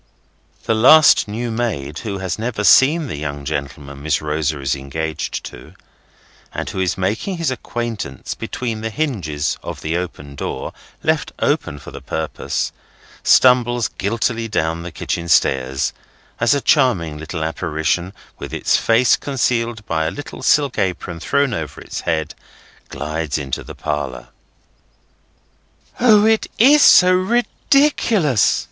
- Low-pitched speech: Yes, very low, 95 Hz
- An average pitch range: No, wide, 8.5 semitones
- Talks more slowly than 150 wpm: Yes, average, 140 wpm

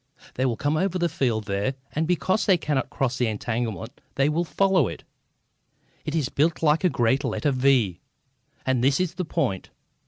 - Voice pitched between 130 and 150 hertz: Yes, medium, 140 Hz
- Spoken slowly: No, average, 185 wpm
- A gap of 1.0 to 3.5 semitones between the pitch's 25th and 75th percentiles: No, average, 5.2 semitones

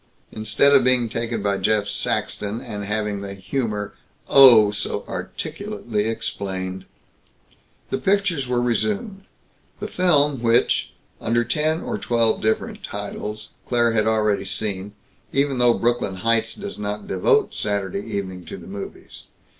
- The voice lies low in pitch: Yes, low, 110 Hz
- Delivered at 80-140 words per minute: Yes, slow, 135 wpm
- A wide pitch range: No, average, 3.8 semitones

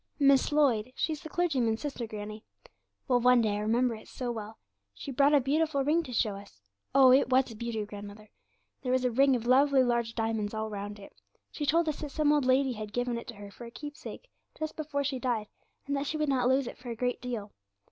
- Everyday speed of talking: No, fast, 235 wpm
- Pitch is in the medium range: No, very high, 250 Hz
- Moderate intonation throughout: Yes, average, 4.1 semitones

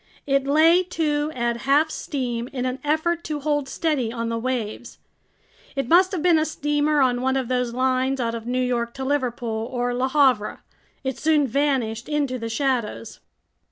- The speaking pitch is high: Yes, very high, 265 Hz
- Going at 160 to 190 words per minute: Yes, average, 180 wpm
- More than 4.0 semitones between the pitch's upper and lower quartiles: No, average, 3.4 semitones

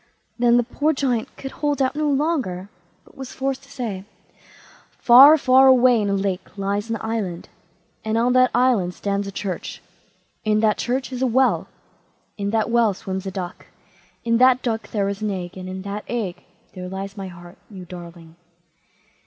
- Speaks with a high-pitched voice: Yes, high, 220 Hz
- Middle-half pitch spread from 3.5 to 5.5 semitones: Yes, average, 4.9 semitones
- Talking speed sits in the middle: Yes, average, 180 wpm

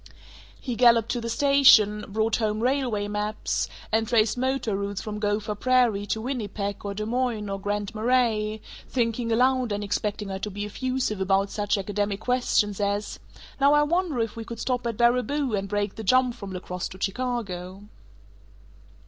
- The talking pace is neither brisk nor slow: Yes, average, 175 wpm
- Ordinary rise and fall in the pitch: Yes, average, 3.3 semitones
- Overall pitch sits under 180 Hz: No, high, 215 Hz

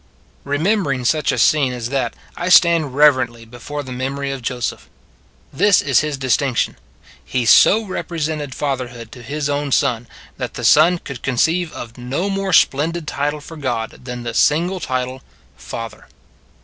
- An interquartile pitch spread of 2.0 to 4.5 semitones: Yes, average, 4.0 semitones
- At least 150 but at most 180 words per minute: Yes, average, 160 wpm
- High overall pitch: No, medium, 140 Hz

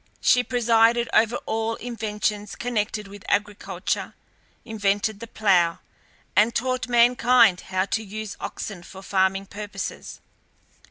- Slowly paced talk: Yes, slow, 115 wpm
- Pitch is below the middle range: No, high, 215 Hz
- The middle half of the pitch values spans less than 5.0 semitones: Yes, average, 2.8 semitones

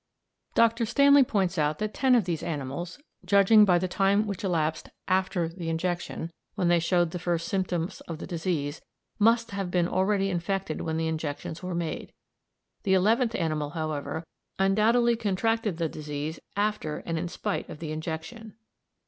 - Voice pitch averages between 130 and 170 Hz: No, medium, 180 Hz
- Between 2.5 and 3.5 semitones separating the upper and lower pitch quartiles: No, average, 4.1 semitones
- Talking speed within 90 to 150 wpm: No, average, 165 wpm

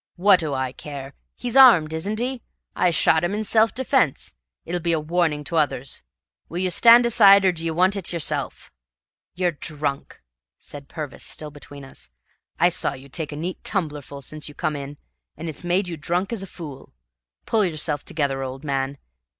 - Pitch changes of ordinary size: Yes, average, 4.4 semitones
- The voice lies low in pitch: No, medium, 160 Hz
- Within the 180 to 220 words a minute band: Yes, average, 185 wpm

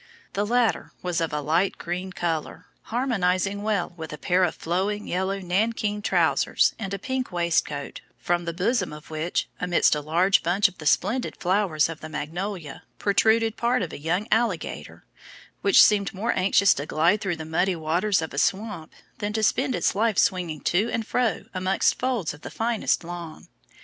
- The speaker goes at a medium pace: Yes, average, 180 wpm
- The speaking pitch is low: No, medium, 185 Hz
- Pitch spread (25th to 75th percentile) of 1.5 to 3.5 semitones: No, average, 4.1 semitones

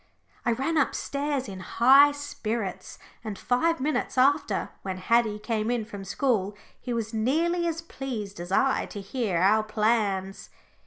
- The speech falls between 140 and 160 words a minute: Yes, average, 150 wpm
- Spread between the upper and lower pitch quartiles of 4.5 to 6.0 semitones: Yes, average, 5.1 semitones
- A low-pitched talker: No, high, 230 Hz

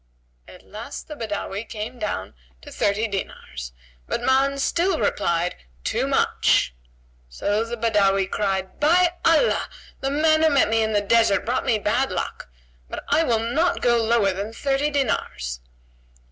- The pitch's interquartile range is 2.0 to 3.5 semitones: No, wide, 5.6 semitones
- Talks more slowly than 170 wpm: Yes, average, 155 wpm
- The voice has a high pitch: Yes, high, 230 Hz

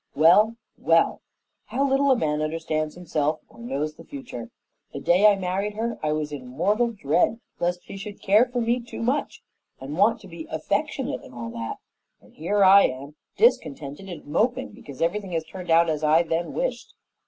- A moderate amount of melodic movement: No, wide, 6.4 semitones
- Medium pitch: Yes, medium, 180 Hz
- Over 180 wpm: Yes, average, 190 wpm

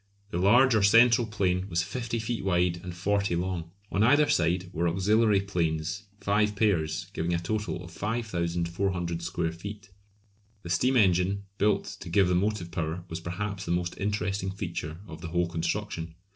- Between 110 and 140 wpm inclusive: No, average, 170 wpm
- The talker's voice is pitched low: Yes, very low, 95 Hz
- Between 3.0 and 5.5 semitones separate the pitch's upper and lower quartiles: Yes, average, 3.3 semitones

